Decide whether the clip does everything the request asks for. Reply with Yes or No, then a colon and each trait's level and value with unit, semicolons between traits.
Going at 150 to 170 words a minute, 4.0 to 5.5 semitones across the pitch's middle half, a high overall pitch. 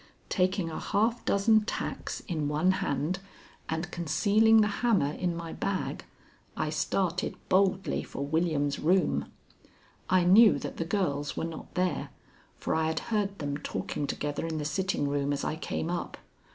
No: average, 160 wpm; average, 4.6 semitones; medium, 170 Hz